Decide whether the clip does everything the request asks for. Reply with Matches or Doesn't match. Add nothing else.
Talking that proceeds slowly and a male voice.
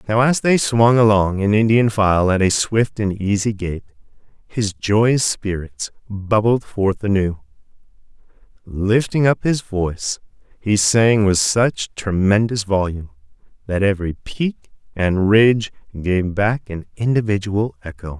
Matches